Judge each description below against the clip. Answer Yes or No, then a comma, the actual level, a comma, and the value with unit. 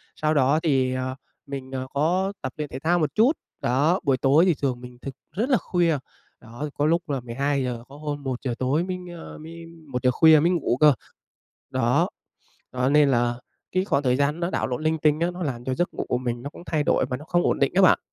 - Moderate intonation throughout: Yes, average, 4.3 semitones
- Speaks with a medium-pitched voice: Yes, medium, 145 Hz